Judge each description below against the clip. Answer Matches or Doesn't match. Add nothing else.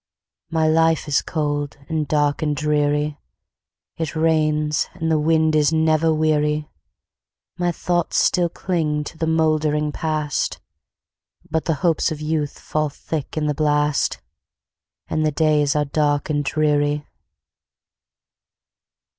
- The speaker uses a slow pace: Matches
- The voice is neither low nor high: Matches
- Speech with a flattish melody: Matches